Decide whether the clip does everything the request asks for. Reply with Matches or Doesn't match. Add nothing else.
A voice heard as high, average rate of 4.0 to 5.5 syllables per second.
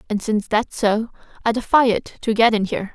Doesn't match